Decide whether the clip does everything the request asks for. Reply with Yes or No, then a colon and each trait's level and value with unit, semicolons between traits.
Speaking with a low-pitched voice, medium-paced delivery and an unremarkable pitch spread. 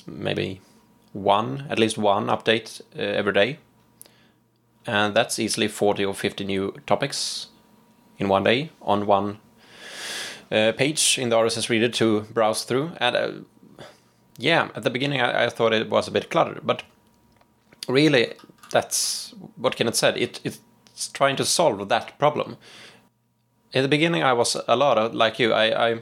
No: low, 115 Hz; average, 165 wpm; narrow, 2.3 semitones